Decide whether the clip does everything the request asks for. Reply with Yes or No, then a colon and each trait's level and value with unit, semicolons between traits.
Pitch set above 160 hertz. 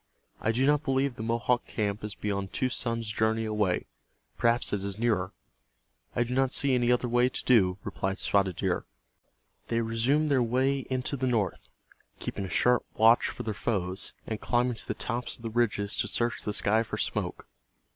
No: low, 115 Hz